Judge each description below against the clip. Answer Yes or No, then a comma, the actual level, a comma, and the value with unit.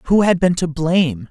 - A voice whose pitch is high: No, medium, 170 Hz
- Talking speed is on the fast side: Yes, fast, 230 wpm